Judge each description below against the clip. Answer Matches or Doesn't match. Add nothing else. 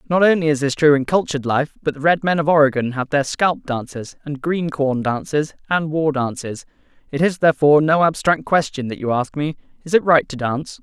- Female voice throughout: Doesn't match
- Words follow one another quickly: Matches